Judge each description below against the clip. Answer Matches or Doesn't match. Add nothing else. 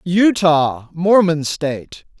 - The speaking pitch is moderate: Matches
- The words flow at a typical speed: Doesn't match